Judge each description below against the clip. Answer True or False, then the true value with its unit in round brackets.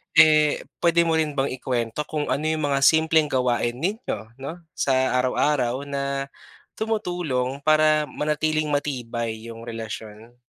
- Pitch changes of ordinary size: True (4.1 semitones)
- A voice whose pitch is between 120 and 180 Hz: True (140 Hz)